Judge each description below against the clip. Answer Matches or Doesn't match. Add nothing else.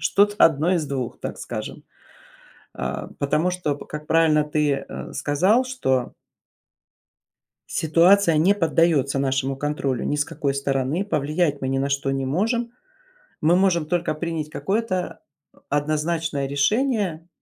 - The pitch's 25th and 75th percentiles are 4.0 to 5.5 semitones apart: Matches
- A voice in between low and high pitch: Matches